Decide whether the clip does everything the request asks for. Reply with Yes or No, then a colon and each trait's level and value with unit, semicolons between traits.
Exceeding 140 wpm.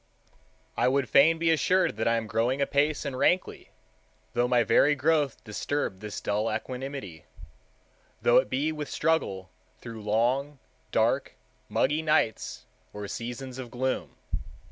No: slow, 135 wpm